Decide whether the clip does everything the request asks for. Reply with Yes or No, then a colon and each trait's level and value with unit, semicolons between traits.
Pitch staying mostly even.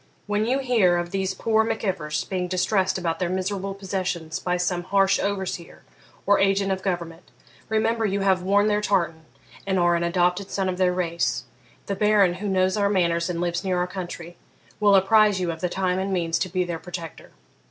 Yes: narrow, 2.1 semitones